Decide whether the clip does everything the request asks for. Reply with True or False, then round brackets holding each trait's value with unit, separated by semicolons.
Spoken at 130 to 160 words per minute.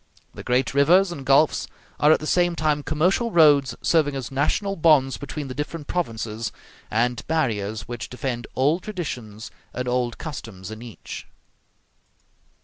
True (145 wpm)